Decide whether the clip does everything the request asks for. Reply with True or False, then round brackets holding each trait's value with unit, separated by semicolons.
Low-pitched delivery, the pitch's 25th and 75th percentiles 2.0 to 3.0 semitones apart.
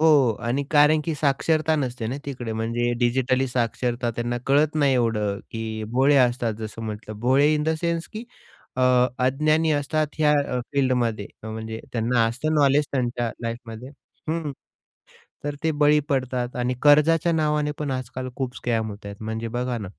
False (130 Hz; 4.1 semitones)